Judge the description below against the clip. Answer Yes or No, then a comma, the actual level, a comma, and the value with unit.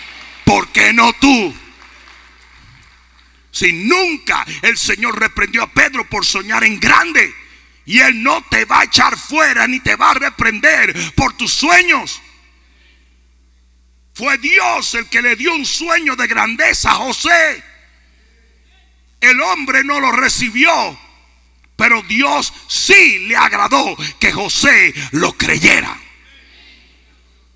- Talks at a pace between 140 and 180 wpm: No, slow, 125 wpm